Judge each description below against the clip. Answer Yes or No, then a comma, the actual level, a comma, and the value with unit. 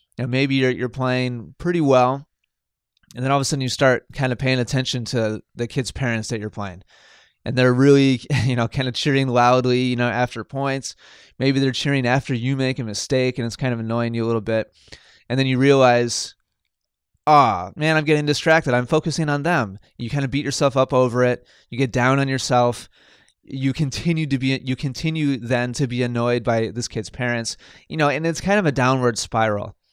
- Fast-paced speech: Yes, fast, 215 wpm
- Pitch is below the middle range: Yes, low, 130 Hz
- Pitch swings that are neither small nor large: No, narrow, 2.2 semitones